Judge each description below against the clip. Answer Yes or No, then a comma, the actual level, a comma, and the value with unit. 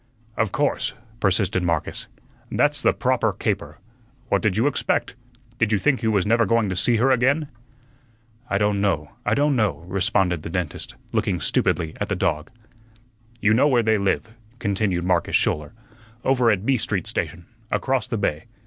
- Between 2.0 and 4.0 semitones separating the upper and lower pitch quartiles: No, average, 4.5 semitones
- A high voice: No, low, 105 Hz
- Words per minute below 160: No, average, 170 wpm